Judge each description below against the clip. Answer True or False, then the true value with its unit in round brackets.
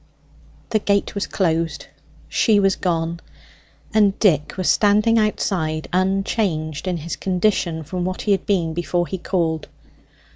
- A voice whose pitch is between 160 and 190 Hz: True (185 Hz)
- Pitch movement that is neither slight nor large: True (3.5 semitones)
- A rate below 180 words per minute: True (140 wpm)